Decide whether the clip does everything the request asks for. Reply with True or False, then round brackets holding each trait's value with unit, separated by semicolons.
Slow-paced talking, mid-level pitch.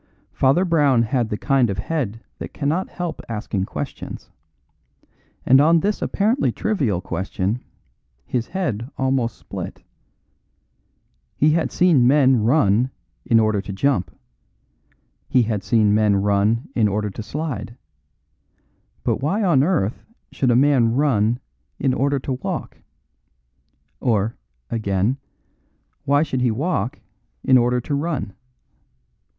False (125 wpm; 125 Hz)